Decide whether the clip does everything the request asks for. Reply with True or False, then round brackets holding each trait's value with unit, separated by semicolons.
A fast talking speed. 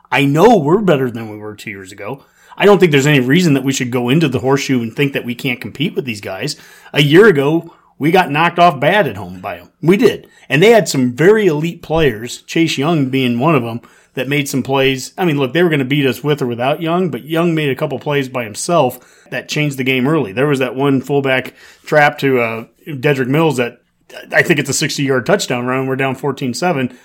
True (245 wpm)